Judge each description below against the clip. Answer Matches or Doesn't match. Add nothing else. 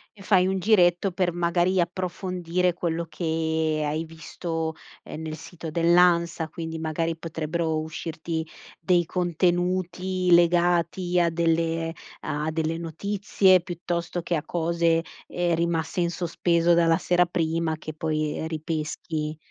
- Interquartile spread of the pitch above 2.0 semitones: Doesn't match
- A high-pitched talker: Doesn't match